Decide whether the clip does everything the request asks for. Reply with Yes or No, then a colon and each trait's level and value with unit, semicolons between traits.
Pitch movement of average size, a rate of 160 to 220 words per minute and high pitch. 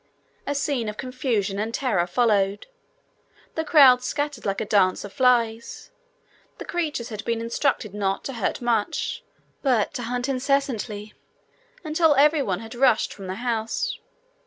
No: average, 4.5 semitones; average, 145 wpm; high, 235 Hz